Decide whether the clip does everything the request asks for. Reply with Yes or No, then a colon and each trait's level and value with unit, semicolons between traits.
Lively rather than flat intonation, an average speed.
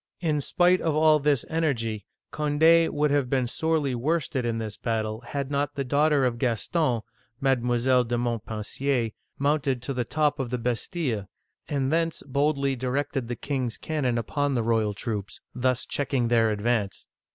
No: average, 3.8 semitones; average, 170 wpm